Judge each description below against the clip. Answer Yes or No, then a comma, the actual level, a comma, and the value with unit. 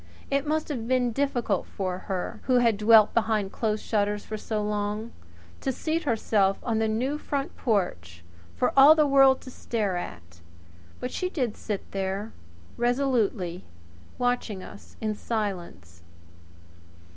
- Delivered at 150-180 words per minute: No, average, 140 wpm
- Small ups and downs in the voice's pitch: No, average, 4.4 semitones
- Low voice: No, high, 220 Hz